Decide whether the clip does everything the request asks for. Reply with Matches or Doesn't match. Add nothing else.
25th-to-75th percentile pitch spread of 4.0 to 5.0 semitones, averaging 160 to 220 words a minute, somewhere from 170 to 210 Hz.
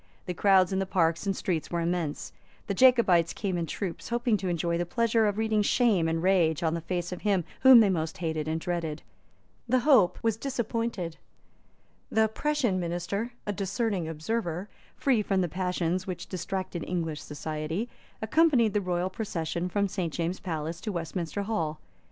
Matches